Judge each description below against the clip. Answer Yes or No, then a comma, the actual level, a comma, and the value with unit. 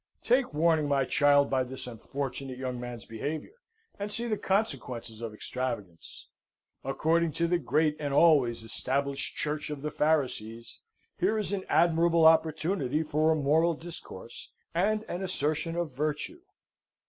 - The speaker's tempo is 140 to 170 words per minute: Yes, average, 145 wpm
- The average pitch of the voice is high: No, medium, 150 Hz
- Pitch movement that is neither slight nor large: Yes, average, 4.4 semitones